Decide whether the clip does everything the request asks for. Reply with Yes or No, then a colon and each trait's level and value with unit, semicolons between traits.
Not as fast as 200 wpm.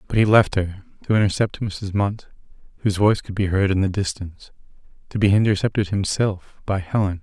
Yes: average, 185 wpm